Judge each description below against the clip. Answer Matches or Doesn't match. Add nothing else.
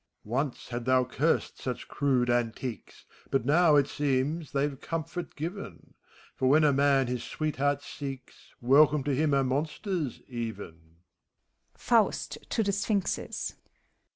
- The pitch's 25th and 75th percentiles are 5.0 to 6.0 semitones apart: Doesn't match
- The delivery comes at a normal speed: Doesn't match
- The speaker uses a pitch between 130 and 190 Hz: Matches